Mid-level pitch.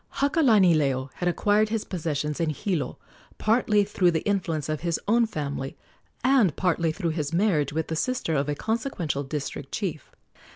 Yes: medium, 170 Hz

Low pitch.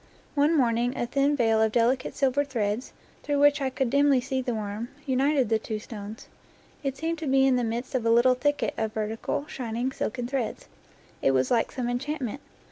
No: very high, 250 Hz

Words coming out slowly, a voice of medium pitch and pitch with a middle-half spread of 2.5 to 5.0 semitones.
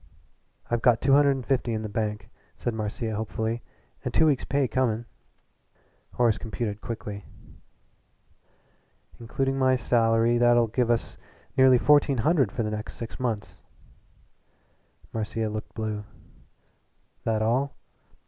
No: slow, 130 wpm; low, 115 Hz; average, 2.9 semitones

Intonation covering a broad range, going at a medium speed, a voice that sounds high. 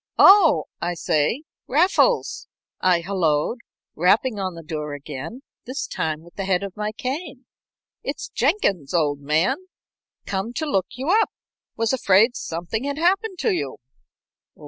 Yes: wide, 8.4 semitones; average, 145 wpm; high, 200 Hz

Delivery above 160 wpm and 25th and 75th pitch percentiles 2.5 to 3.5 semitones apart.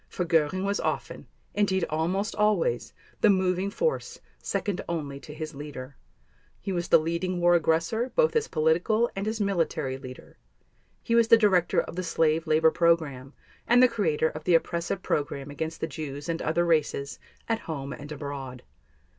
No: average, 170 wpm; average, 4.6 semitones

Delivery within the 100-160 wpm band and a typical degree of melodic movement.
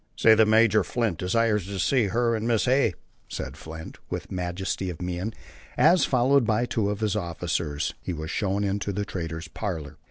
No: average, 185 wpm; average, 4.3 semitones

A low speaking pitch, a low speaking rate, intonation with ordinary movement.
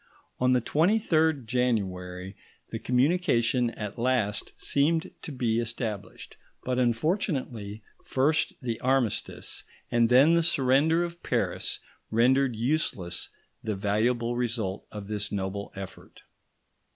Yes: low, 120 Hz; slow, 115 wpm; average, 4.6 semitones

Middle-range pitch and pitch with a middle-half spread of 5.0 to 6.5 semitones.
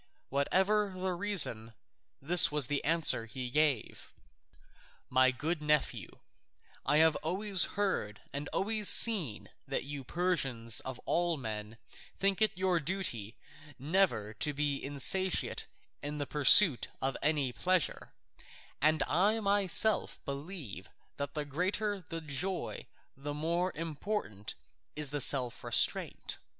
Yes: medium, 150 Hz; wide, 5.4 semitones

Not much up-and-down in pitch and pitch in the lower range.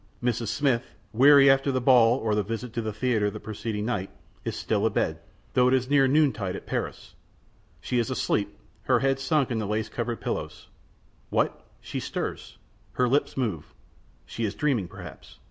No: average, 3.6 semitones; low, 120 Hz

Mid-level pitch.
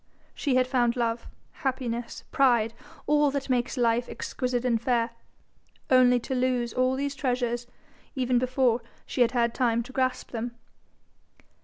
No: very high, 250 Hz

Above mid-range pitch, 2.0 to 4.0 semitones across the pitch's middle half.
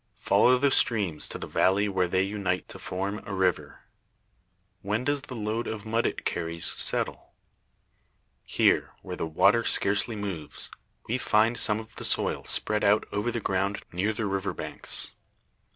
No: low, 105 Hz; average, 3.0 semitones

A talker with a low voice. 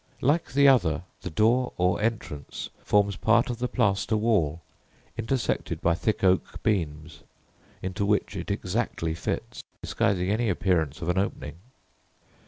Yes: low, 100 Hz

